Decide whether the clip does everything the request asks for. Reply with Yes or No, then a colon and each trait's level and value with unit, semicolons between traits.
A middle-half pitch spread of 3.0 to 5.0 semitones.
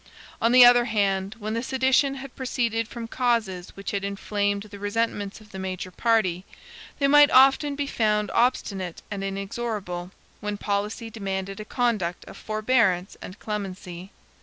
Yes: average, 3.5 semitones